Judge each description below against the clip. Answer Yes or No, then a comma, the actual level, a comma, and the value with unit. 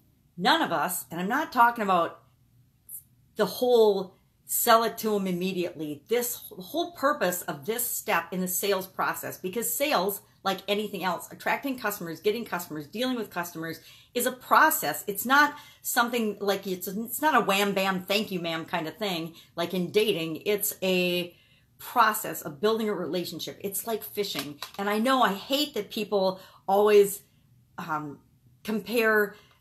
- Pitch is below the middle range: No, high, 195 Hz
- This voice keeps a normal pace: Yes, average, 160 wpm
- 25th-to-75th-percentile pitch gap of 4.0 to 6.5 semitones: Yes, average, 4.7 semitones